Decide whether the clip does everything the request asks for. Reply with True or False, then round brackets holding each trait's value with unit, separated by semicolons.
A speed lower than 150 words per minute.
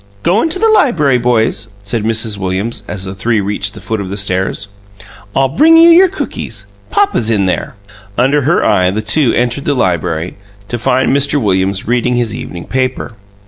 False (185 wpm)